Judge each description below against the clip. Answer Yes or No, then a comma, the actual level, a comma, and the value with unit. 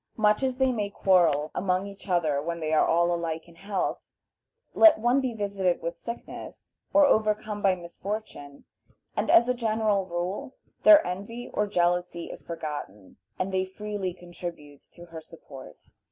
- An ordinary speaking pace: Yes, average, 155 wpm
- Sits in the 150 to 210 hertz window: Yes, medium, 185 Hz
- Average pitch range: Yes, average, 4.0 semitones